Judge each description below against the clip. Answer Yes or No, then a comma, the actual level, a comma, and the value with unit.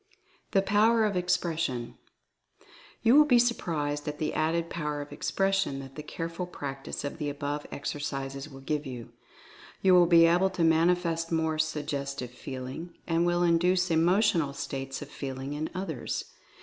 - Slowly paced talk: No, average, 160 wpm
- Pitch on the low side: No, medium, 160 Hz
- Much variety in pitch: No, average, 3.8 semitones